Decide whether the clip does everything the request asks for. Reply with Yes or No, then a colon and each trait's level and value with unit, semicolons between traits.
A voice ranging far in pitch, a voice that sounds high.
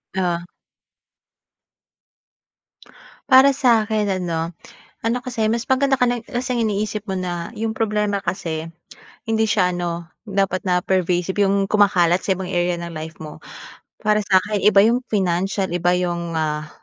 No: average, 3.9 semitones; high, 195 Hz